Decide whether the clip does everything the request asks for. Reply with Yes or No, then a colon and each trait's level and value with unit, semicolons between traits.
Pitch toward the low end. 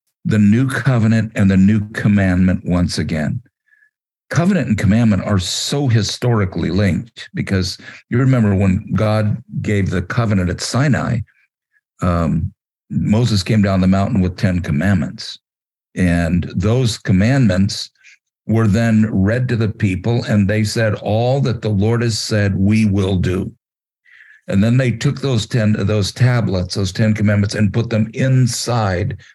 Yes: low, 105 Hz